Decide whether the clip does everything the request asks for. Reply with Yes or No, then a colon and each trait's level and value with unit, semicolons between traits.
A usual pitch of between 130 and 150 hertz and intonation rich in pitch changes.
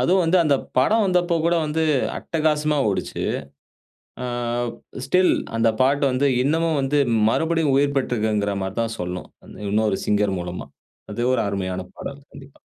Yes: medium, 140 Hz; wide, 7.2 semitones